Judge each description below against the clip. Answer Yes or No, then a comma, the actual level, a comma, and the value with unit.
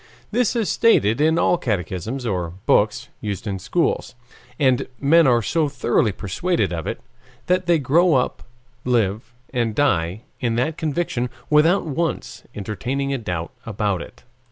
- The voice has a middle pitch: No, low, 125 Hz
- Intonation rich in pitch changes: Yes, wide, 7.3 semitones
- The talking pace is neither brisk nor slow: Yes, average, 150 wpm